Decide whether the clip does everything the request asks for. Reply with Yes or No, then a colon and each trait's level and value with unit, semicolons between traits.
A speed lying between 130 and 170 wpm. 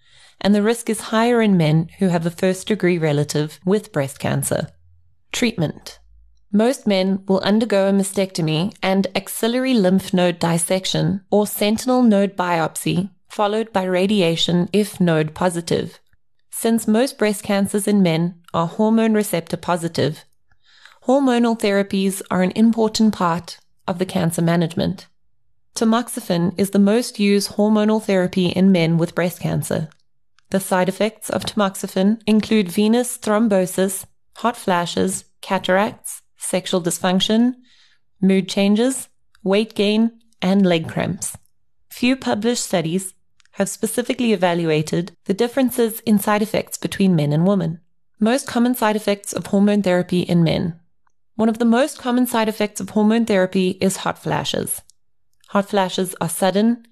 Yes: average, 140 wpm